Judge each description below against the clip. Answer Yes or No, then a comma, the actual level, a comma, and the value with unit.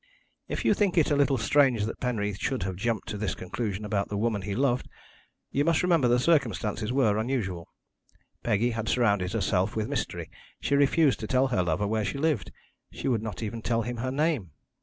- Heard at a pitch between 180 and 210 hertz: No, low, 115 Hz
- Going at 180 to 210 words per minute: Yes, average, 200 wpm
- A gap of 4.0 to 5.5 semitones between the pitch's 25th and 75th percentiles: Yes, average, 4.5 semitones